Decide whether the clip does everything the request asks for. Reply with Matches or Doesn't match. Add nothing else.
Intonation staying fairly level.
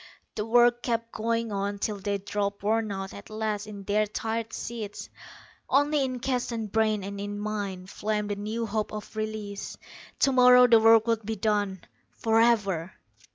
Matches